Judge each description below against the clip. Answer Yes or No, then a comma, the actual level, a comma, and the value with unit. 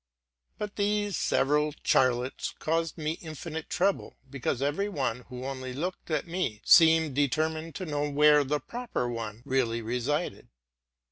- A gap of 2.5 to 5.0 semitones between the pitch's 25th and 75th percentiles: Yes, average, 4.1 semitones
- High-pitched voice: No, medium, 150 Hz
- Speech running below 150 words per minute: Yes, average, 140 wpm